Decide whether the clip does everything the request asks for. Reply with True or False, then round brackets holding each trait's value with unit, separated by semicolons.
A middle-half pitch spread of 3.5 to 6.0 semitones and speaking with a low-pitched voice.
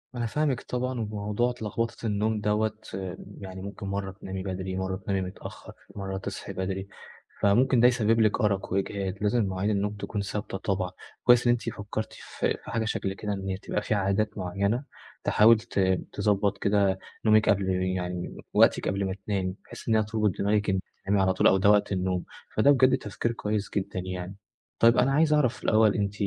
False (2.4 semitones; 100 Hz)